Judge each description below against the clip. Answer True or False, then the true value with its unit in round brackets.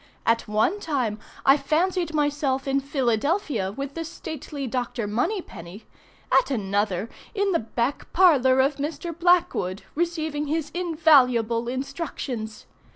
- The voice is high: True (275 Hz)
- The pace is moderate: False (120 wpm)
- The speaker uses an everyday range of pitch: False (5.7 semitones)